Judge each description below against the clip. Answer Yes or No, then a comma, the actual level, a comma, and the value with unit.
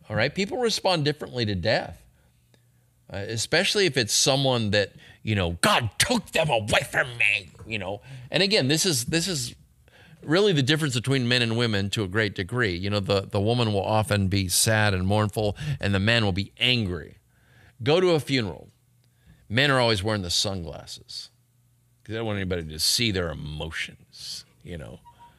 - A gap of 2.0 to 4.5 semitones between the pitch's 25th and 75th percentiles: No, average, 5.0 semitones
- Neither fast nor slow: Yes, average, 185 wpm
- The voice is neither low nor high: No, low, 115 Hz